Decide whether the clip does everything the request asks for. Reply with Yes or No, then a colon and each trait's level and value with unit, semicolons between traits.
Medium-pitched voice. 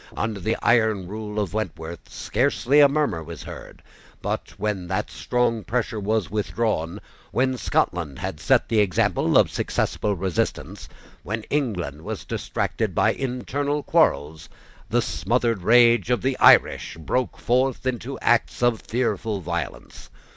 No: low, 110 Hz